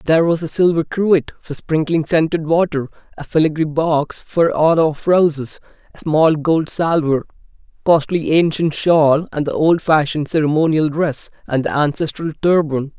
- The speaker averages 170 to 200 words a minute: No, average, 150 wpm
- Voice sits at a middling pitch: Yes, medium, 155 Hz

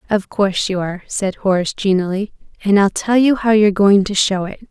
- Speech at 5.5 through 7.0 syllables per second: Yes, 5.8 syllables/s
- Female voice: Yes, female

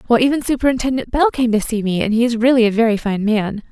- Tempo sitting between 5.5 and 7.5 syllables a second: Yes, 6.4 syllables/s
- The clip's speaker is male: No, female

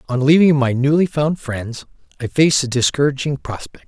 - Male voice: Yes, male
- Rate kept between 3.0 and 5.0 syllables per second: No, 5.4 syllables/s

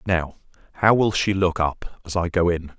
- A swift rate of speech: Yes, fast, 215 wpm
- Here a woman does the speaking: No, male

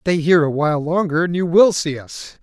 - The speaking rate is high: Yes, fast, 245 wpm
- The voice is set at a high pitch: No, medium, 165 Hz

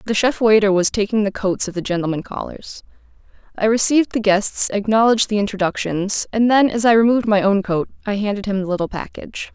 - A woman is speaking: Yes, female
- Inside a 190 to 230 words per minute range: Yes, average, 200 wpm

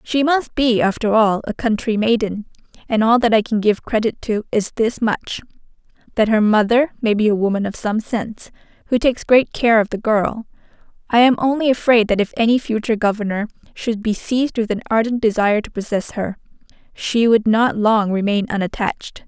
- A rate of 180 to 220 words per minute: Yes, average, 190 wpm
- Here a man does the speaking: No, female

